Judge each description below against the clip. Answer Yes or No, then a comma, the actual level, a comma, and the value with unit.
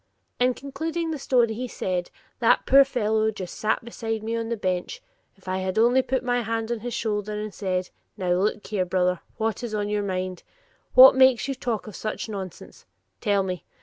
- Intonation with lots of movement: No, average, 4.3 semitones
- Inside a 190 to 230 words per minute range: Yes, average, 195 wpm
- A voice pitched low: No, high, 220 Hz